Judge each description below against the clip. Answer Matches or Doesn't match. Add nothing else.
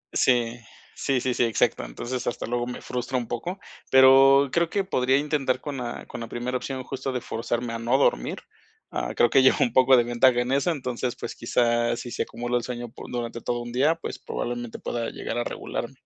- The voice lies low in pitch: Matches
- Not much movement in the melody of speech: Matches